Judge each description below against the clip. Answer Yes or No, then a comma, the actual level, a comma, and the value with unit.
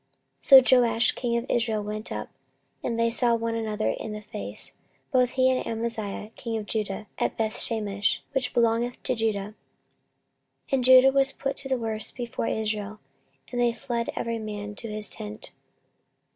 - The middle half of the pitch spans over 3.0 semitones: No, narrow, 2.4 semitones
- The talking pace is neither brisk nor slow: Yes, average, 175 wpm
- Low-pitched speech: No, high, 230 Hz